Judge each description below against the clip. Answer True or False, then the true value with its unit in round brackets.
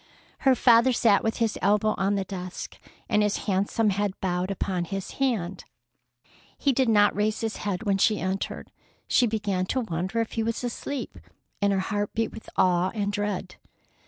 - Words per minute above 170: True (180 wpm)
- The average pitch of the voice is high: True (205 Hz)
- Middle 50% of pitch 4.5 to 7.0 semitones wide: False (2.8 semitones)